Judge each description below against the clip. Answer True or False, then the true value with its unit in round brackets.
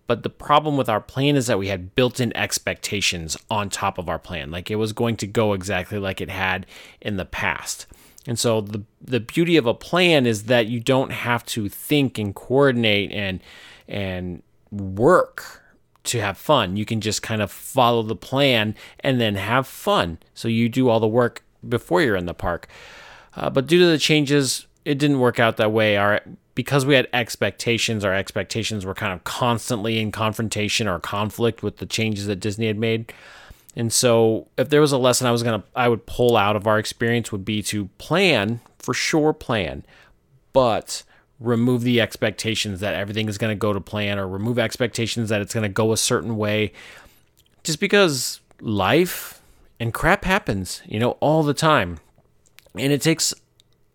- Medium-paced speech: True (190 wpm)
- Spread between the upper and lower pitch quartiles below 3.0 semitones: False (3.5 semitones)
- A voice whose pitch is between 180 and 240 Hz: False (115 Hz)